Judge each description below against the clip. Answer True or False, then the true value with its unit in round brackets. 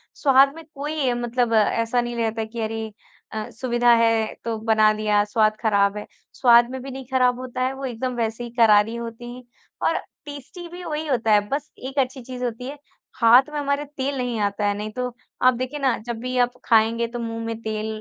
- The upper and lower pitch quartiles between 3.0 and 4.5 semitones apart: False (2.6 semitones)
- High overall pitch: True (240 Hz)